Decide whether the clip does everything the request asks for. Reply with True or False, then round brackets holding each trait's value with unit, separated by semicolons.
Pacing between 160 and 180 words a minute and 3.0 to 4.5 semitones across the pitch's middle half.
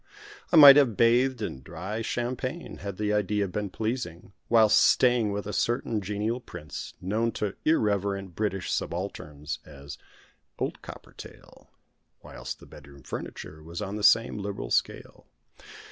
False (140 wpm; 4.1 semitones)